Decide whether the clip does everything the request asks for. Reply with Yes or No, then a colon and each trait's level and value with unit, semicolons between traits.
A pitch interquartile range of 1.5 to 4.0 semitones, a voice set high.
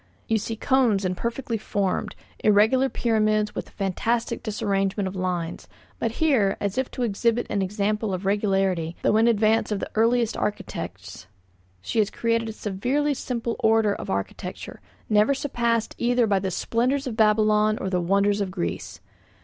Yes: average, 2.9 semitones; high, 215 Hz